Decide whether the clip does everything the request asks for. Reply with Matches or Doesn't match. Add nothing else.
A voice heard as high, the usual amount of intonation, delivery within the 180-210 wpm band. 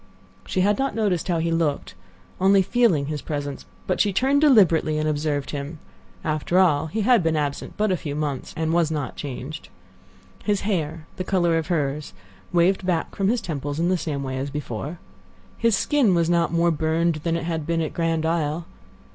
Doesn't match